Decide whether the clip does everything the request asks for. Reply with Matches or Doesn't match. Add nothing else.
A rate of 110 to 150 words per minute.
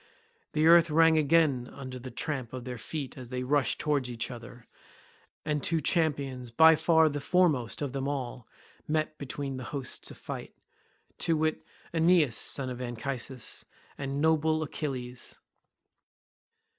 Matches